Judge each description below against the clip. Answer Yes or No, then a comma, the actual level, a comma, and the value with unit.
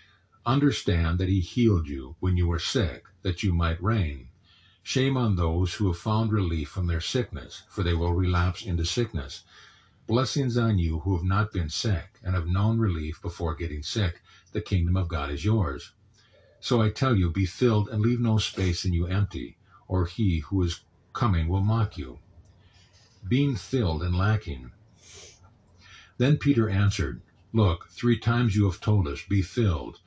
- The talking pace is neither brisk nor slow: Yes, average, 175 wpm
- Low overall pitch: Yes, very low, 95 Hz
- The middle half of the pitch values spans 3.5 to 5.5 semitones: Yes, average, 4.0 semitones